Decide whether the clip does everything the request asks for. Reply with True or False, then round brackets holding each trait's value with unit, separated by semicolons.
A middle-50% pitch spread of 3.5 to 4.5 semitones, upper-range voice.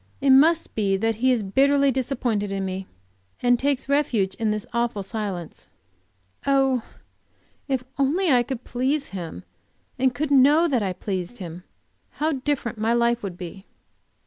False (5.5 semitones; 240 Hz)